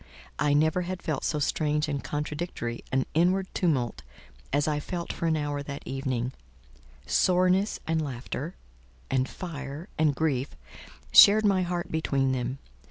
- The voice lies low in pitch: No, medium, 150 Hz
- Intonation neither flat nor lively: Yes, average, 4.1 semitones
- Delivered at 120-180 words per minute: Yes, average, 145 wpm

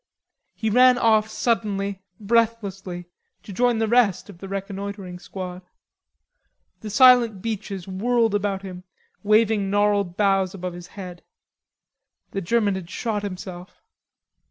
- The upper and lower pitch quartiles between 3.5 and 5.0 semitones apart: No, average, 2.8 semitones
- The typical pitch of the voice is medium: No, high, 200 Hz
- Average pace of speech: No, slow, 125 wpm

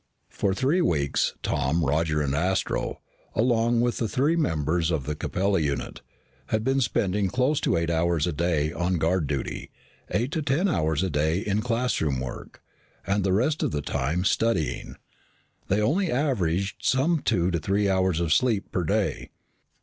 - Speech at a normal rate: Yes, average, 170 wpm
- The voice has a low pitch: Yes, very low, 95 Hz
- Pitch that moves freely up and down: Yes, wide, 6.8 semitones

